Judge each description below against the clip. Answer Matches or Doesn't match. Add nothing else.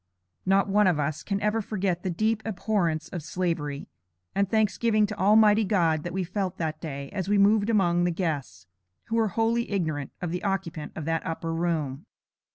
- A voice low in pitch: Doesn't match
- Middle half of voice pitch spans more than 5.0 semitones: Doesn't match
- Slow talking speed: Doesn't match